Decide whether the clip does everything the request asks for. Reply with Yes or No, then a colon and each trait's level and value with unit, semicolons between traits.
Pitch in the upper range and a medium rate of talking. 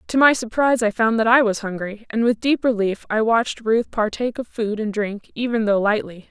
No: high, 225 Hz; fast, 230 wpm